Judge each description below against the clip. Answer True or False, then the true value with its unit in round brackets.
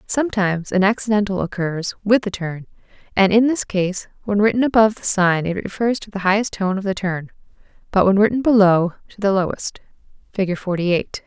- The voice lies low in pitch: False (200 Hz)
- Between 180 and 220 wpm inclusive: True (185 wpm)